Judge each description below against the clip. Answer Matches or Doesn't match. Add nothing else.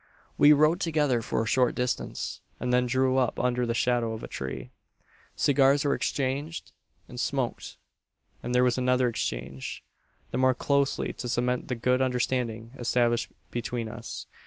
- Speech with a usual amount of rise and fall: Doesn't match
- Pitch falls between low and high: Doesn't match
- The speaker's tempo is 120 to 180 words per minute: Matches